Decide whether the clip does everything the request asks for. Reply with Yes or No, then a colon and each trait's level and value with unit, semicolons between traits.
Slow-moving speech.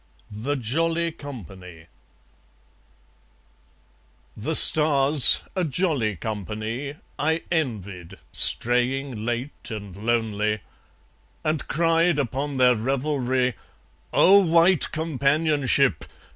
Yes: slow, 80 wpm